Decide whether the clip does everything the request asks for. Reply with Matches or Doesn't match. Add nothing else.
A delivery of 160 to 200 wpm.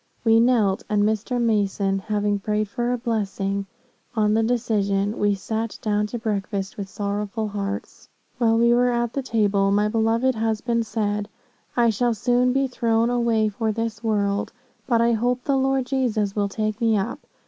Matches